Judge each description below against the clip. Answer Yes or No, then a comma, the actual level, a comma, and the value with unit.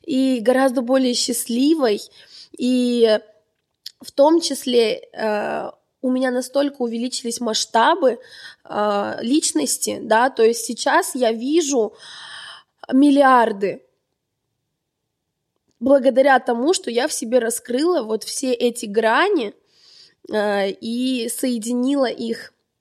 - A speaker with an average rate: No, slow, 100 wpm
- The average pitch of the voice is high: Yes, very high, 250 Hz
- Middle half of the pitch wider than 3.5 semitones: No, average, 2.9 semitones